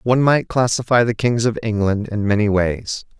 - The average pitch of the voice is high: No, low, 110 Hz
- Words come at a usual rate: Yes, average, 190 wpm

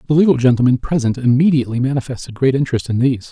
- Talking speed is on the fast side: No, average, 180 wpm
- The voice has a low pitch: Yes, low, 130 Hz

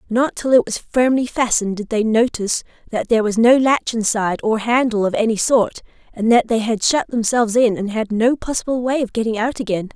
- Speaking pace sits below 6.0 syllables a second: Yes, 5.7 syllables/s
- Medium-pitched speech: No, high, 230 Hz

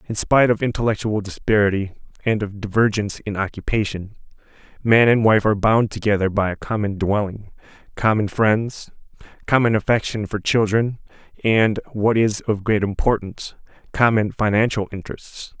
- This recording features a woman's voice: No, male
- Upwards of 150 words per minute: No, slow, 135 wpm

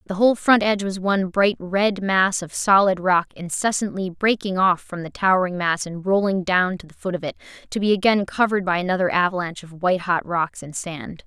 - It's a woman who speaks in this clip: Yes, female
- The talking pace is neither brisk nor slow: No, fast, 215 wpm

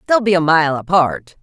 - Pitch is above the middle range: No, medium, 165 Hz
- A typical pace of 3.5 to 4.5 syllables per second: No, 5.0 syllables/s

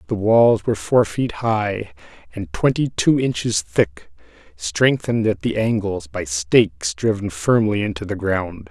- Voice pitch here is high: No, low, 110 Hz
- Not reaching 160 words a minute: Yes, average, 150 wpm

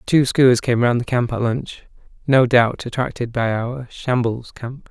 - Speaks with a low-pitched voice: Yes, low, 125 Hz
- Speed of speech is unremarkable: Yes, average, 185 wpm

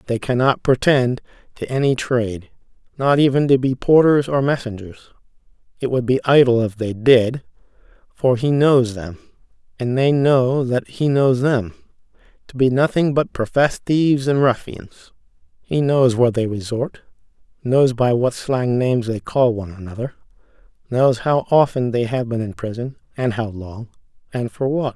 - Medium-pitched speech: No, low, 125 Hz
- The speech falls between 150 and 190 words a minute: Yes, average, 160 wpm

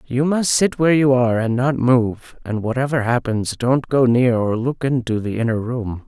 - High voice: No, low, 125 Hz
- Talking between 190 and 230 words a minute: Yes, fast, 205 wpm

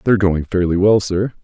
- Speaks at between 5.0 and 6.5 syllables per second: Yes, 5.6 syllables/s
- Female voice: No, male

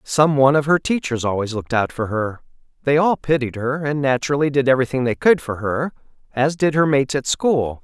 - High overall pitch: No, low, 135 Hz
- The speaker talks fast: Yes, fast, 215 wpm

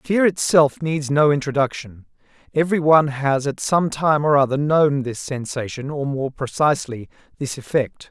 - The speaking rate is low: No, average, 150 wpm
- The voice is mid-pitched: Yes, medium, 145 Hz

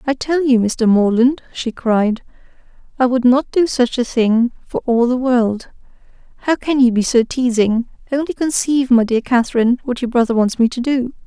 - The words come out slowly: No, average, 190 wpm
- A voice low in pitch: No, high, 245 Hz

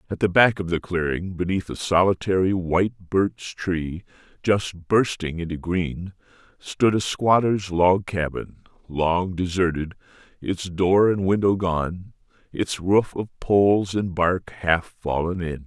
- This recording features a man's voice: Yes, male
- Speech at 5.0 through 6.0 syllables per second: No, 3.9 syllables/s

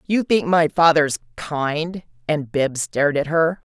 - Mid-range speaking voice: Yes, medium, 155 Hz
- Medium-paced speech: Yes, average, 160 wpm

